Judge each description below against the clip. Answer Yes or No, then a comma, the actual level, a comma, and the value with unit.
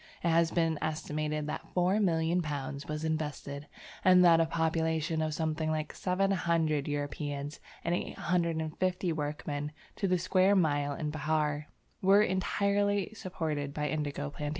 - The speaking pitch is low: No, medium, 160 Hz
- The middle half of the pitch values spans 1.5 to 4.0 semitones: Yes, average, 3.0 semitones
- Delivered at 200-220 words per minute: No, average, 140 wpm